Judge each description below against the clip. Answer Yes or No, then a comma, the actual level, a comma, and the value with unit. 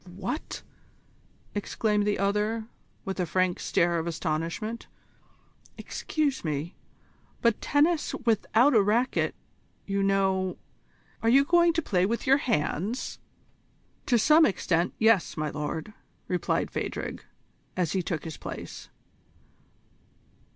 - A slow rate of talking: Yes, slow, 115 wpm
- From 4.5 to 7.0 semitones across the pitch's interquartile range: Yes, average, 4.9 semitones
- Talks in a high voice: Yes, high, 200 Hz